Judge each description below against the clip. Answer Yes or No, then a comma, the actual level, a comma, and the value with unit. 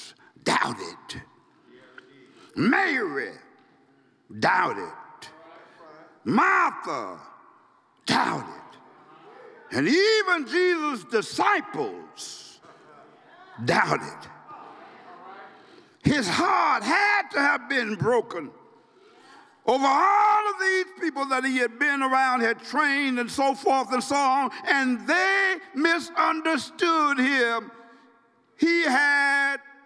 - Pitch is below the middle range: No, very high, 300 Hz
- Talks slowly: Yes, slow, 80 wpm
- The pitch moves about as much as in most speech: No, wide, 6.7 semitones